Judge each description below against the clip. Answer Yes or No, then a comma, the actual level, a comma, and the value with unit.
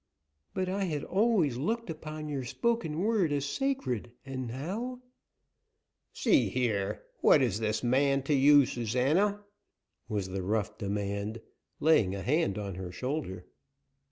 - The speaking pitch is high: No, low, 135 Hz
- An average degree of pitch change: No, wide, 8.0 semitones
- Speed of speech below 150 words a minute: Yes, average, 140 wpm